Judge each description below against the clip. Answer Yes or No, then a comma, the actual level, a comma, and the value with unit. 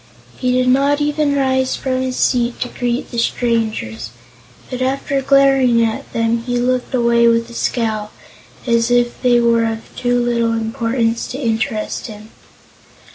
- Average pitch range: No, narrow, 1.9 semitones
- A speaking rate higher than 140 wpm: Yes, average, 155 wpm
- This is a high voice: Yes, high, 240 Hz